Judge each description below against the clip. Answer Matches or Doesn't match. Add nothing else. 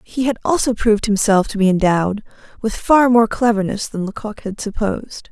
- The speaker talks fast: Doesn't match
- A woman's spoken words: Matches